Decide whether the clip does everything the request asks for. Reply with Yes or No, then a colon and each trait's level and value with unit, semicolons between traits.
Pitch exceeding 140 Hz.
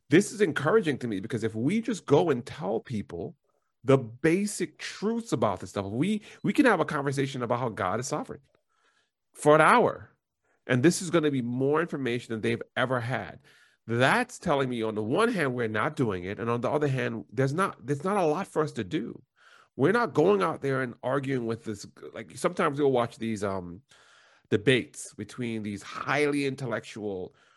No: low, 135 Hz